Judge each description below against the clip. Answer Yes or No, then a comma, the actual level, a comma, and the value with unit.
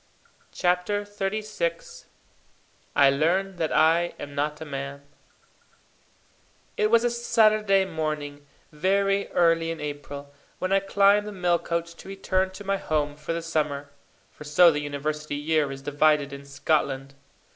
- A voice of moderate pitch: Yes, medium, 165 Hz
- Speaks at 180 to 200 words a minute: No, average, 145 wpm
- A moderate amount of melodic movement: Yes, average, 5.0 semitones